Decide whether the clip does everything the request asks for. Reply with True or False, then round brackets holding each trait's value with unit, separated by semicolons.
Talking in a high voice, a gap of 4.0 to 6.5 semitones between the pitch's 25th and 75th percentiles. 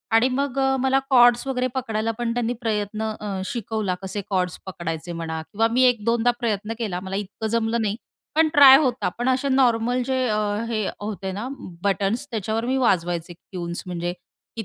True (225 Hz; 4.3 semitones)